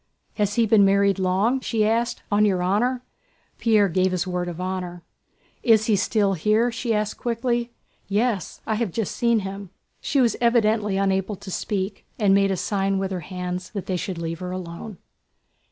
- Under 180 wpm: No, average, 185 wpm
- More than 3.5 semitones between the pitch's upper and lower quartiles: No, average, 3.2 semitones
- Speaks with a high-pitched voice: Yes, high, 200 Hz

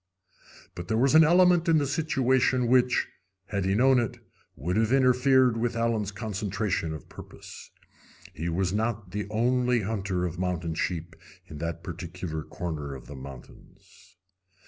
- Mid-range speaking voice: No, low, 105 Hz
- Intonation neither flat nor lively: No, wide, 6.4 semitones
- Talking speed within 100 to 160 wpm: Yes, average, 150 wpm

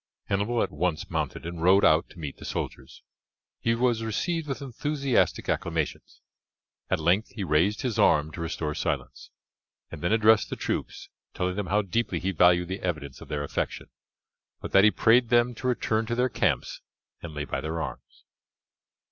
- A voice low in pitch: Yes, very low, 95 Hz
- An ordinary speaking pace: Yes, average, 180 wpm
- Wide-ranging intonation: Yes, wide, 6.0 semitones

